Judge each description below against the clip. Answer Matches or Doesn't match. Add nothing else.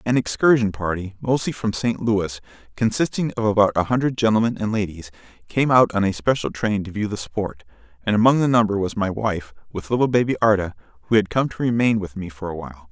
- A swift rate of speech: Matches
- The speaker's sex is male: Matches